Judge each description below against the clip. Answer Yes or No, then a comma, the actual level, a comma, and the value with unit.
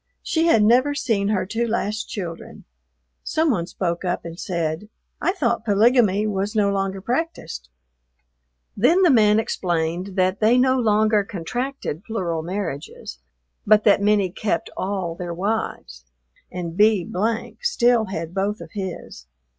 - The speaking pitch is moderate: No, high, 205 Hz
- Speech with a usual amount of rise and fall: Yes, average, 4.2 semitones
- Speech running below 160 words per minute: Yes, average, 140 wpm